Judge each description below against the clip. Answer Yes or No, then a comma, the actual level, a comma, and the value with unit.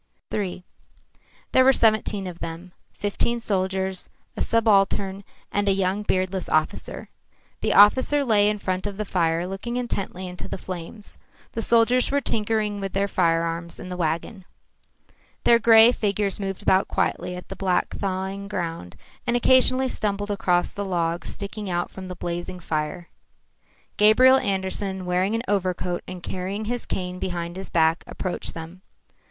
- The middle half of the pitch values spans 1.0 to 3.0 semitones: Yes, average, 2.7 semitones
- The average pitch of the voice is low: No, high, 190 Hz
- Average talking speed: Yes, average, 155 wpm